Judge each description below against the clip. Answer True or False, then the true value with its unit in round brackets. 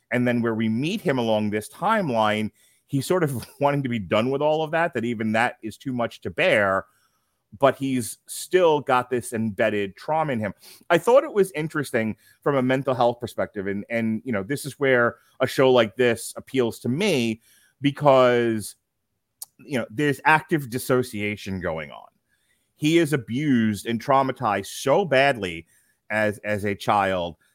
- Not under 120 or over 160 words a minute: False (175 wpm)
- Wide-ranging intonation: False (4.2 semitones)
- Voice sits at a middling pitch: False (125 Hz)